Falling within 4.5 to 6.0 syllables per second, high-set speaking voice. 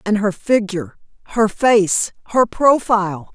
No: 4.2 syllables/s; high, 210 Hz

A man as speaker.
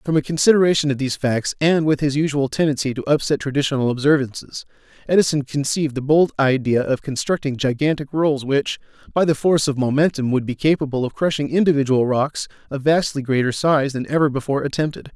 Yes: male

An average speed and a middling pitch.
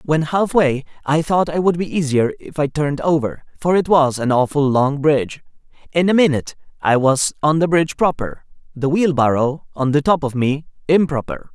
Yes: average, 190 wpm; medium, 150 Hz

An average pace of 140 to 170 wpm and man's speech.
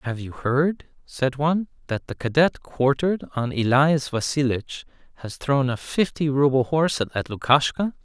Yes: average, 150 wpm; male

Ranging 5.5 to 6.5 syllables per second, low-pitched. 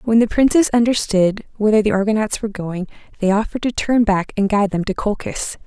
No: 6.0 syllables/s; high, 210 Hz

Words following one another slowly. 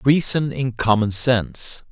Yes: slow, 125 wpm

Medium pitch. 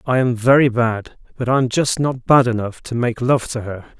No: low, 120 Hz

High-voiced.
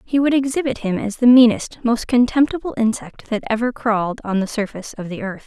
Yes: high, 230 Hz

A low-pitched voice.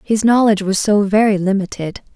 No: high, 205 Hz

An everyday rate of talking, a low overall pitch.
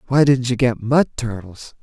Yes: average, 195 wpm; low, 125 Hz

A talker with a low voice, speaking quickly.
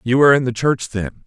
Yes: low, 125 Hz; fast, 285 wpm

